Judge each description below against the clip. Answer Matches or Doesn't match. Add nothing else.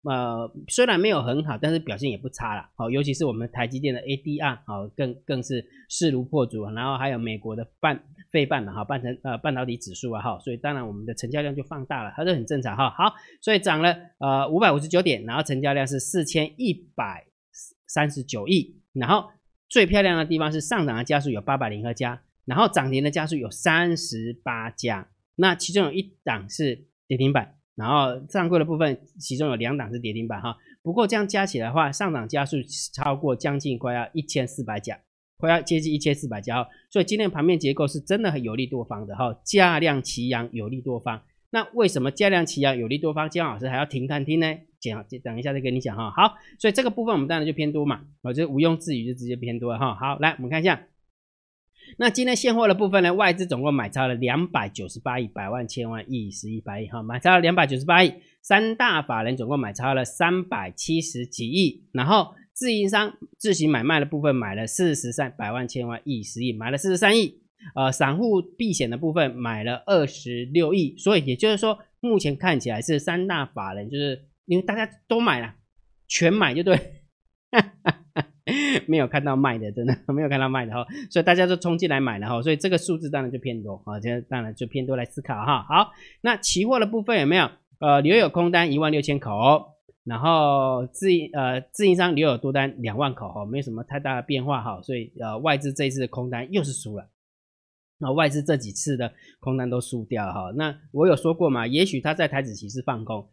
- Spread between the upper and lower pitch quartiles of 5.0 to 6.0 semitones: Matches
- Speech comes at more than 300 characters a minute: Matches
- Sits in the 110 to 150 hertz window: Matches